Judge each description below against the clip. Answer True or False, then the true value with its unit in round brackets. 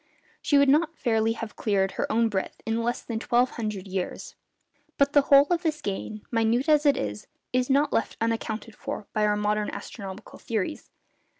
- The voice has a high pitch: True (225 Hz)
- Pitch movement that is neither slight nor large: True (4.7 semitones)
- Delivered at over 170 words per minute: True (185 wpm)